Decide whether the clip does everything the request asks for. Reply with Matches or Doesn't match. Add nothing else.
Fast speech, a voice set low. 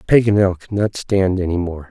Doesn't match